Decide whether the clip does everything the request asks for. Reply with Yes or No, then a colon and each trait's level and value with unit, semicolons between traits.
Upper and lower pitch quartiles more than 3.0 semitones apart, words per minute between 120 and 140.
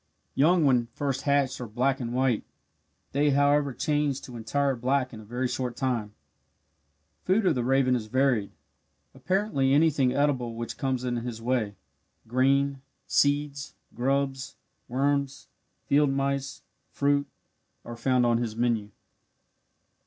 No: narrow, 2.6 semitones; slow, 135 wpm